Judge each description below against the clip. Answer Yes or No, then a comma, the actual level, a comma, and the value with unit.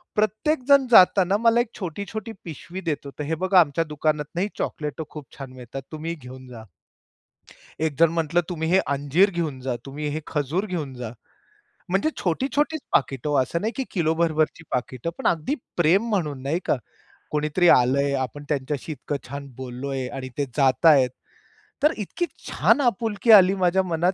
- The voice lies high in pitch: No, medium, 160 Hz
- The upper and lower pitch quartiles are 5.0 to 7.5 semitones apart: Yes, average, 5.3 semitones